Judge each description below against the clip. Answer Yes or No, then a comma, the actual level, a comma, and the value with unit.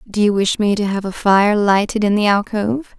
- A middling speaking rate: No, fast, 240 wpm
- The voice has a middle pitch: No, high, 205 Hz